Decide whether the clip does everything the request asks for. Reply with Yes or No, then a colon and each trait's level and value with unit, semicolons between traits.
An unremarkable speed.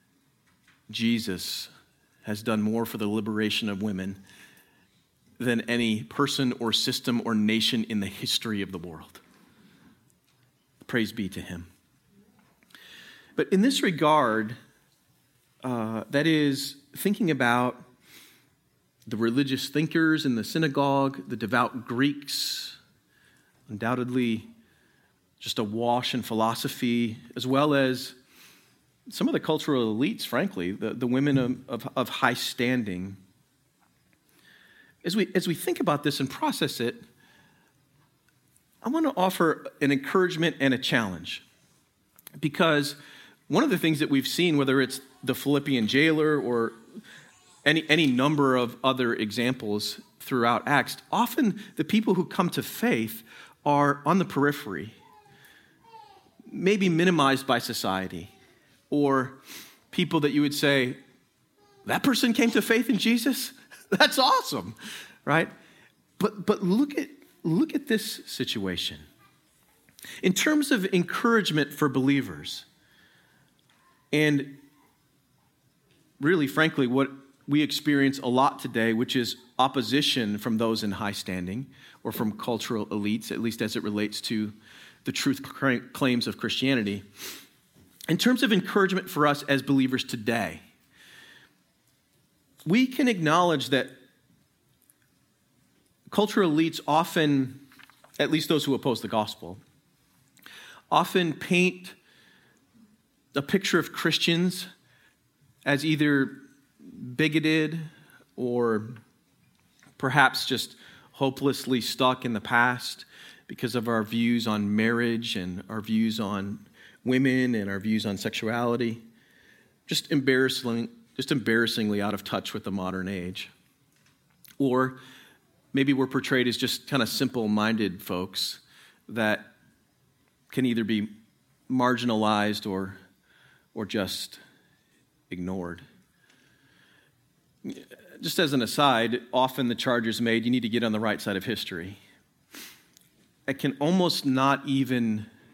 No: slow, 120 wpm